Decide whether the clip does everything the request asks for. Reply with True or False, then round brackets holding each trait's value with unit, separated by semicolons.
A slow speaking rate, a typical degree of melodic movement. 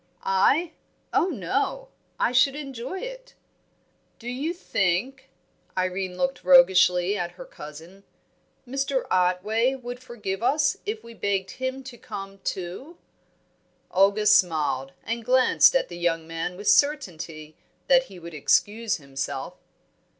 False (130 wpm; 6.8 semitones)